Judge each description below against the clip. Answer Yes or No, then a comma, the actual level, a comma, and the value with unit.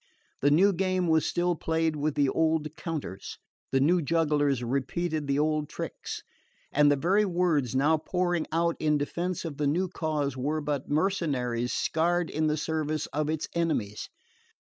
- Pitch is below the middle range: No, medium, 155 Hz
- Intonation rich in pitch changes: No, average, 2.8 semitones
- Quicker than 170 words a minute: No, average, 165 wpm